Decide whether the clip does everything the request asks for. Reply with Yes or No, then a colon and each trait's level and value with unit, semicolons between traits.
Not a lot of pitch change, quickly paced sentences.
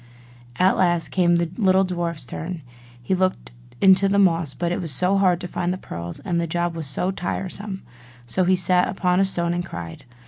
Yes: narrow, 1.8 semitones; fast, 215 wpm